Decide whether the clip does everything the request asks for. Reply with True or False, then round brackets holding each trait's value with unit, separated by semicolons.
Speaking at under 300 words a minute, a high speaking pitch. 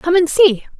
True (225 wpm; 330 Hz)